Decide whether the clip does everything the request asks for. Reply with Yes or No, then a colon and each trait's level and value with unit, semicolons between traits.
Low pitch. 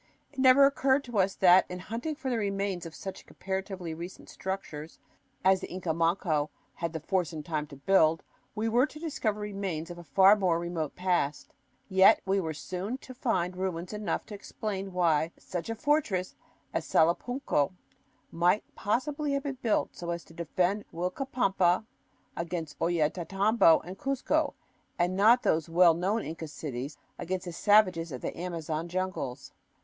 No: medium, 185 Hz